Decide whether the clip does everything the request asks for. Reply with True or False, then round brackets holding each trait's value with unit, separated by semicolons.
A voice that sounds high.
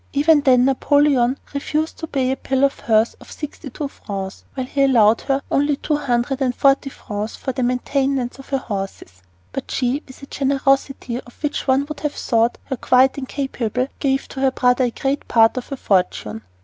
True (265 Hz)